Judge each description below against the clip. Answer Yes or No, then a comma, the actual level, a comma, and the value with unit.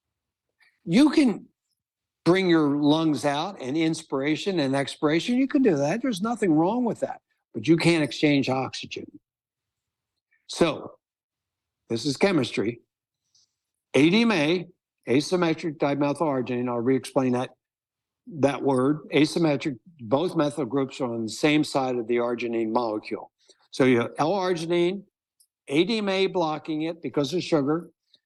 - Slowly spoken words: Yes, slow, 125 wpm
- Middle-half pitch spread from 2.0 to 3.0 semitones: No, average, 5.1 semitones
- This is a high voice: No, medium, 150 Hz